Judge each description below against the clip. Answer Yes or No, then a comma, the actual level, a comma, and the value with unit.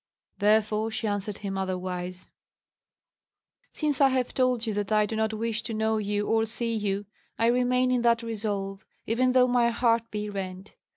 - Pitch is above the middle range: Yes, high, 220 Hz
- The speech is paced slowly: No, average, 175 wpm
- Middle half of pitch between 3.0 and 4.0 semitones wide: No, narrow, 2.5 semitones